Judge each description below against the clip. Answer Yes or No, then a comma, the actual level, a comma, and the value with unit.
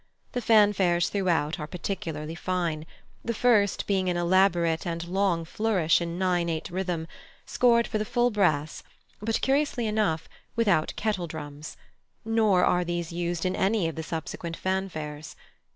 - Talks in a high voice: No, medium, 180 Hz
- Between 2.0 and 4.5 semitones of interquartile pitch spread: Yes, average, 3.8 semitones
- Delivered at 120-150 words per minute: Yes, average, 145 wpm